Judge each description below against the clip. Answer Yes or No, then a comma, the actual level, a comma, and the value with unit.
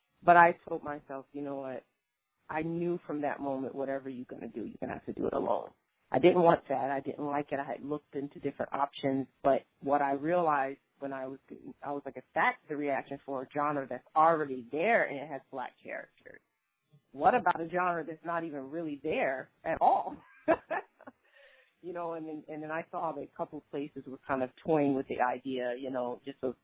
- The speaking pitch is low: No, medium, 145 Hz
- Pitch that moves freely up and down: No, average, 3.3 semitones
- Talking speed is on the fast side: Yes, fast, 225 wpm